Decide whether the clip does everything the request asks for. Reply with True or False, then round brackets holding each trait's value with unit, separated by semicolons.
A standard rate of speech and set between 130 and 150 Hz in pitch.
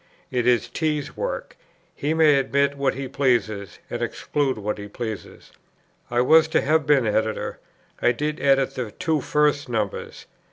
True (160 wpm; 135 Hz)